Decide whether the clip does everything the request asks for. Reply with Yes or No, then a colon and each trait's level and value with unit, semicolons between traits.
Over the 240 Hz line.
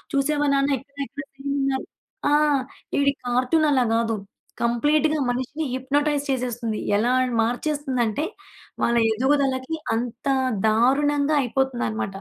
Yes: very high, 270 Hz